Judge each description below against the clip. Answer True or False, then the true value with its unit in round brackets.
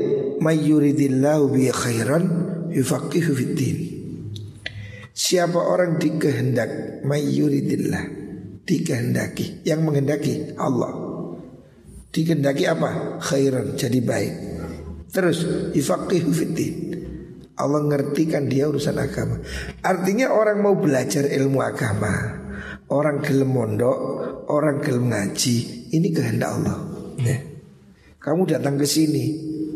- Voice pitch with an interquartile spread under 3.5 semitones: False (3.9 semitones)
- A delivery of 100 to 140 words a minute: False (85 wpm)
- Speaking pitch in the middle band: True (145 Hz)